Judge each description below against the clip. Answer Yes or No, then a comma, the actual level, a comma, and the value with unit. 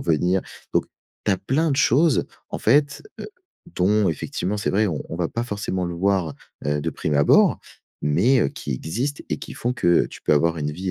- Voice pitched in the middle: No, very low, 95 Hz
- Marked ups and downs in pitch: Yes, wide, 6.4 semitones